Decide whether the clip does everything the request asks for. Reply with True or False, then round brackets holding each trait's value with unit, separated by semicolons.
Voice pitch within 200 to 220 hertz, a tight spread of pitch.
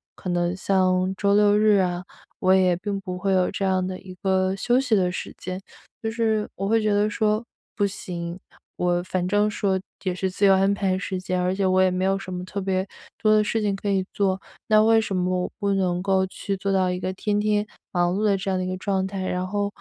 False (190 Hz; 1.9 semitones)